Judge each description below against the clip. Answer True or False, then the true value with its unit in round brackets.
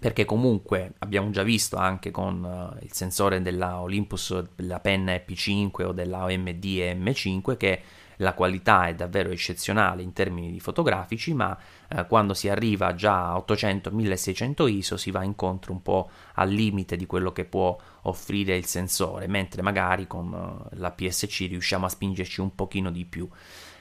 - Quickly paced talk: False (155 wpm)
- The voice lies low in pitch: True (95 Hz)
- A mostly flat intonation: True (1.8 semitones)